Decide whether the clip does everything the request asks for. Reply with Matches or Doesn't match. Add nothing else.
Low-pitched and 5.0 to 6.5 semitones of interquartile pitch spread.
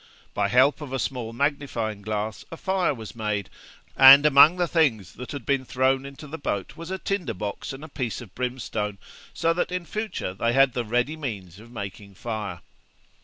Matches